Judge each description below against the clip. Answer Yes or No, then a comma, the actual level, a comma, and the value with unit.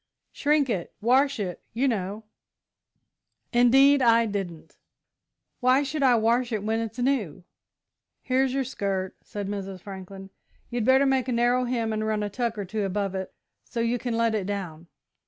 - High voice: Yes, high, 225 Hz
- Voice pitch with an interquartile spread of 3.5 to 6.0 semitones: Yes, average, 4.2 semitones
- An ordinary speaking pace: Yes, average, 170 wpm